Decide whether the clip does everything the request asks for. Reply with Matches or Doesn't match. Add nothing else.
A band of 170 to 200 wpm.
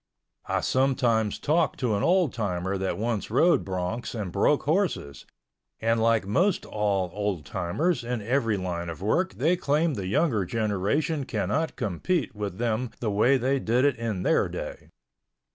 Doesn't match